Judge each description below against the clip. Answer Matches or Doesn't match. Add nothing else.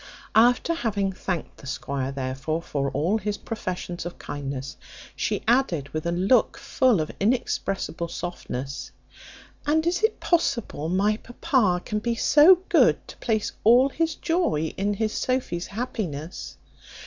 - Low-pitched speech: Doesn't match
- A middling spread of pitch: Doesn't match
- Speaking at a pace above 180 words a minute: Doesn't match